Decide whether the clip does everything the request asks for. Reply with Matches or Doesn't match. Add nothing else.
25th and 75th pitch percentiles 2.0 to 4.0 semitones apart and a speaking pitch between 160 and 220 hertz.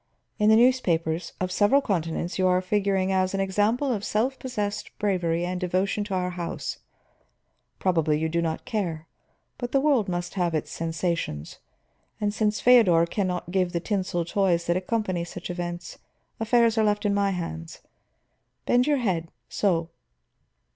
Matches